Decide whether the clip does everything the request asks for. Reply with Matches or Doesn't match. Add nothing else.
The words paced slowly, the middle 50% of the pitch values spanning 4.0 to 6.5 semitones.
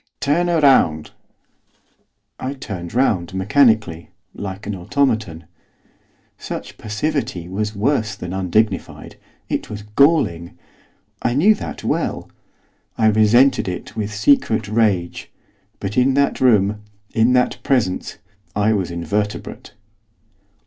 Matches